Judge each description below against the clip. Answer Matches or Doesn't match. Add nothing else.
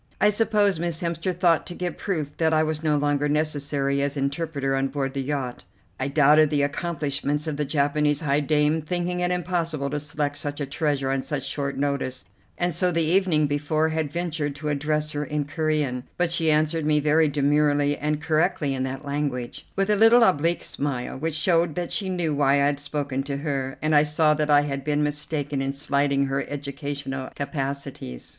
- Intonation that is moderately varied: Doesn't match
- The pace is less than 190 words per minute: Doesn't match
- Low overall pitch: Doesn't match